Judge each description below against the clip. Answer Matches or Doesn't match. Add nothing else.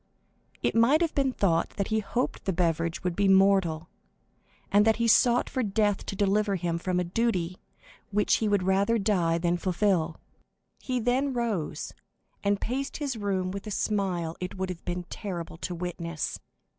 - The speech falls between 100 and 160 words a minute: Doesn't match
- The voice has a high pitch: Matches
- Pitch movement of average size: Matches